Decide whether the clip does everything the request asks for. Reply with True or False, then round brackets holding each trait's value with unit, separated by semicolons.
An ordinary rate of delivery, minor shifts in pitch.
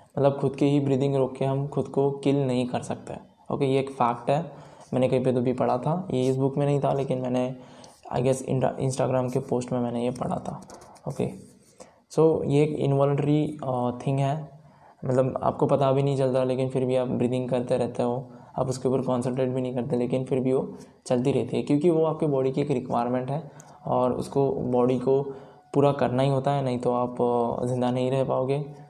False (220 wpm; 1.7 semitones)